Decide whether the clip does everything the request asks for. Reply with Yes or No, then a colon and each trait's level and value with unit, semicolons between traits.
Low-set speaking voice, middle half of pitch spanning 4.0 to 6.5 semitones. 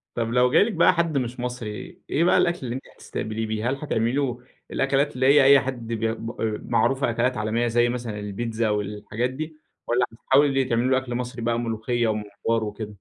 No: low, 120 Hz; average, 2.9 semitones